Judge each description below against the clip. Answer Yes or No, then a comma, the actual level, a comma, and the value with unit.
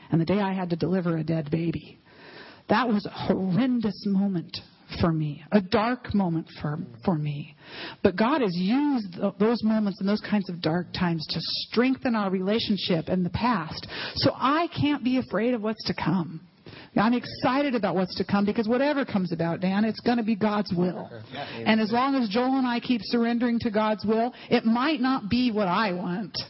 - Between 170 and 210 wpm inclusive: Yes, average, 195 wpm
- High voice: Yes, high, 205 Hz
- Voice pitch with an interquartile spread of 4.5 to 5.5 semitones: Yes, average, 5.1 semitones